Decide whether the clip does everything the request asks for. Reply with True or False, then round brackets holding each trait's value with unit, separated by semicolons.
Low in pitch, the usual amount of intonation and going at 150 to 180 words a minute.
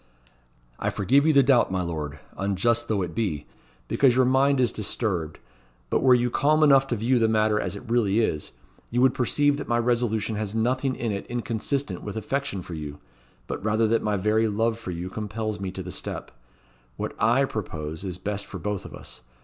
False (110 Hz; 4.0 semitones; 205 wpm)